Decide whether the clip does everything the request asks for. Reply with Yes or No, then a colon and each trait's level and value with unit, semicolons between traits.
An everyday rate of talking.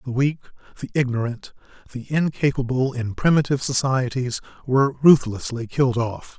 No: slow, 120 wpm